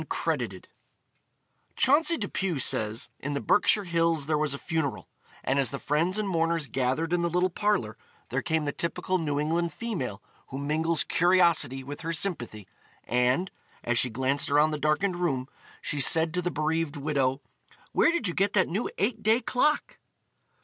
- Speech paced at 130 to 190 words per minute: Yes, average, 170 wpm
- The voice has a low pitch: No, medium, 160 Hz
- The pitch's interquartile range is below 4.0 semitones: No, average, 4.5 semitones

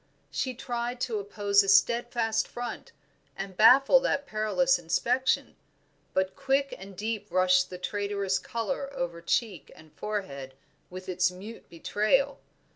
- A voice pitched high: Yes, high, 210 Hz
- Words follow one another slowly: Yes, slow, 130 wpm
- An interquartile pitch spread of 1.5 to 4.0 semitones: No, average, 4.6 semitones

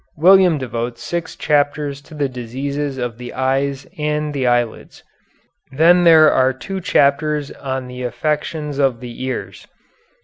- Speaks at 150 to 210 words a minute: No, slow, 135 wpm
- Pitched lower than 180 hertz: Yes, medium, 140 Hz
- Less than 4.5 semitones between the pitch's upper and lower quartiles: Yes, average, 2.8 semitones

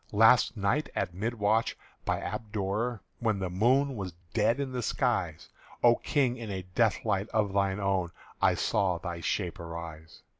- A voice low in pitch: Yes, low, 105 Hz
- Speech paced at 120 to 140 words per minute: No, average, 165 wpm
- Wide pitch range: No, average, 3.8 semitones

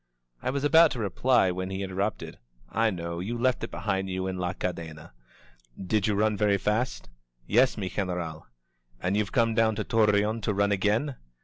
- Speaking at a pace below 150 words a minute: No, average, 185 wpm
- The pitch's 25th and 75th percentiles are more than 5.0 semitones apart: No, average, 3.3 semitones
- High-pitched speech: No, low, 105 Hz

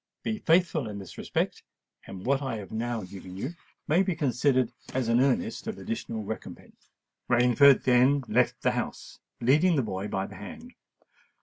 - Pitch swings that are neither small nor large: No, wide, 5.9 semitones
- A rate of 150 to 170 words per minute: Yes, average, 165 wpm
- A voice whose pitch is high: No, low, 125 Hz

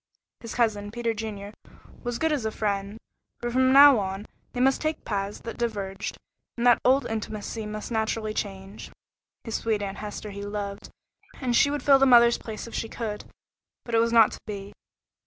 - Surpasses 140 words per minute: Yes, average, 190 wpm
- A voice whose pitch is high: Yes, high, 220 Hz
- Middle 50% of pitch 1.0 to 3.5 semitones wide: Yes, average, 2.7 semitones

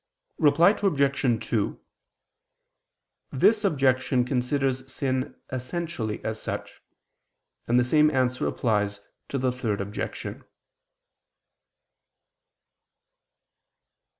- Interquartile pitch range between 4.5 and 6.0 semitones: No, narrow, 2.6 semitones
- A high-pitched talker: No, low, 130 Hz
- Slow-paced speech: Yes, slow, 80 wpm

